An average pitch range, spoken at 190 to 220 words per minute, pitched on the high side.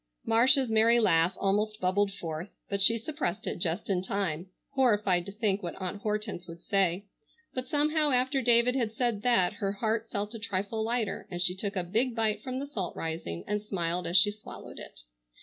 Yes: average, 3.8 semitones; average, 195 wpm; high, 210 Hz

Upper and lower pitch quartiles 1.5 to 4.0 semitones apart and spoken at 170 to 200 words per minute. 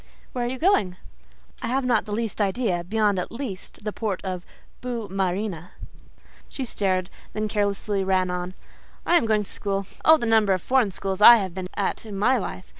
Yes: average, 3.5 semitones; average, 190 wpm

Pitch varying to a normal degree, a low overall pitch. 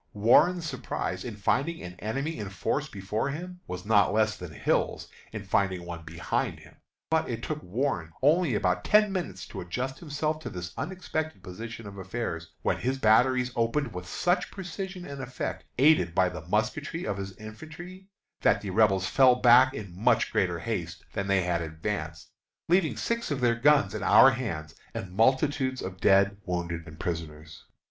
No: wide, 7.7 semitones; low, 110 Hz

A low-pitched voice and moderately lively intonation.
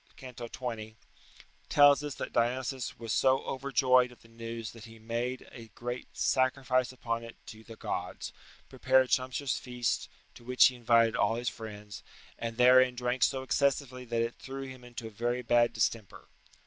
No: low, 120 Hz; narrow, 1.9 semitones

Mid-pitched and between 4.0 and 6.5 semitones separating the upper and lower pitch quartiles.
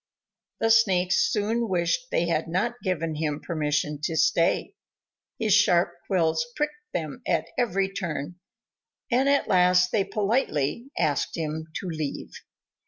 Yes: medium, 180 Hz; average, 5.2 semitones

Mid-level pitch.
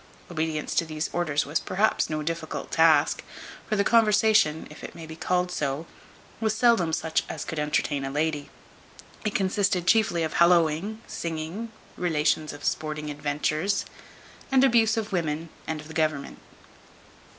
Yes: medium, 160 Hz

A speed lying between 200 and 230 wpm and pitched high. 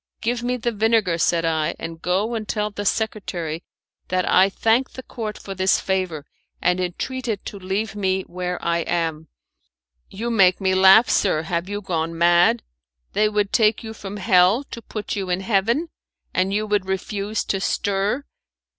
No: average, 175 wpm; high, 195 Hz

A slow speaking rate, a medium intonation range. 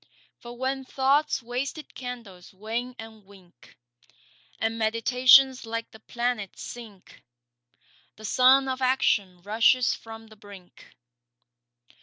Yes: slow, 110 wpm; average, 3.2 semitones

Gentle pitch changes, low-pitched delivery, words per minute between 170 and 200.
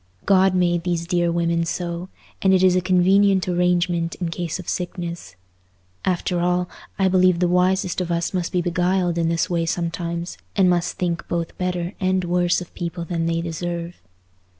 No: narrow, 1.3 semitones; medium, 175 Hz; average, 175 wpm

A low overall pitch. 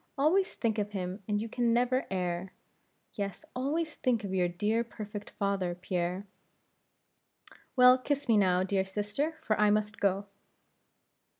No: high, 210 Hz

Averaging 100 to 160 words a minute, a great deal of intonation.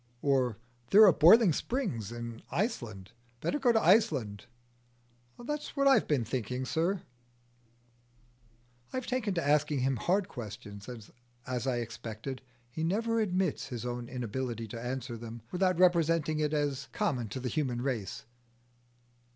Yes: average, 145 wpm; wide, 7.6 semitones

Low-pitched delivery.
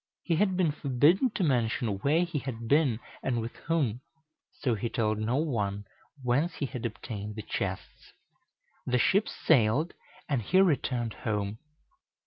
Yes: low, 125 Hz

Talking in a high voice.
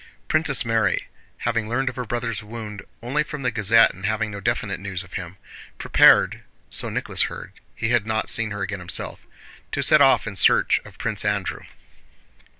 No: low, 110 Hz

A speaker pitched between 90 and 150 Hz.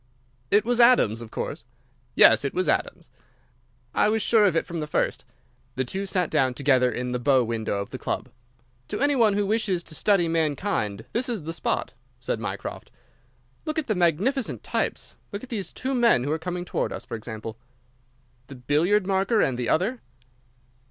No: medium, 175 Hz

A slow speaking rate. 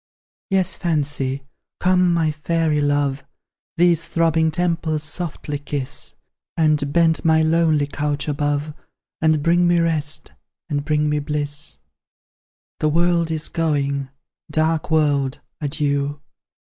Yes: slow, 115 wpm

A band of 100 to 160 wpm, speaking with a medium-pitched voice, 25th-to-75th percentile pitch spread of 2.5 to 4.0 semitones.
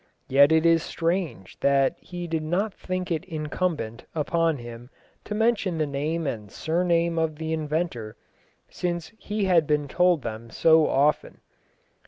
Yes: average, 150 wpm; medium, 160 Hz; average, 3.6 semitones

